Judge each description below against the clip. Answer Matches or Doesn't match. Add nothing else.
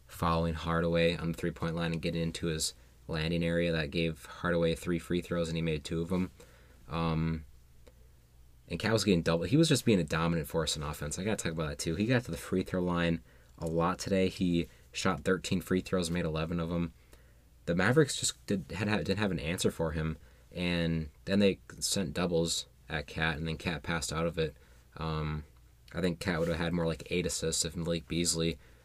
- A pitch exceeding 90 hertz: Doesn't match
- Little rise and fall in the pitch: Matches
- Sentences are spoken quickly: Matches